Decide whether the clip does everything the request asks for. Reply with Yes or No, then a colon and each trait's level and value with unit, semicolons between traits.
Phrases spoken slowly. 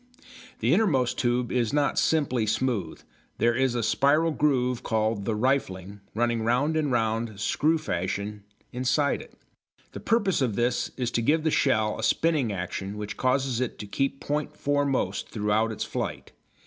No: average, 160 wpm